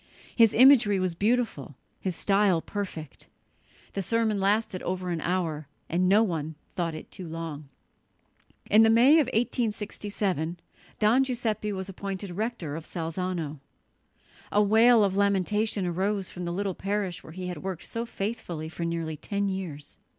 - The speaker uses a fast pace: No, average, 150 wpm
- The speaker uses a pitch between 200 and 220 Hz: No, high, 190 Hz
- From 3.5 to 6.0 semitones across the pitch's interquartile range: Yes, average, 3.9 semitones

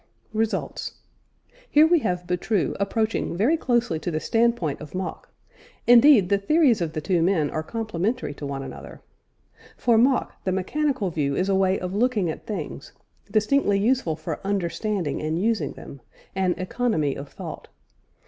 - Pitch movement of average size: No, wide, 5.7 semitones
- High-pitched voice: Yes, high, 195 Hz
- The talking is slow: No, average, 160 wpm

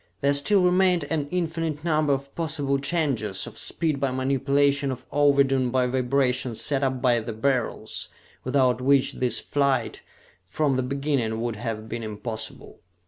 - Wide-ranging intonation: No, narrow, 2.6 semitones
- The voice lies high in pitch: No, low, 135 Hz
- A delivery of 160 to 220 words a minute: No, average, 150 wpm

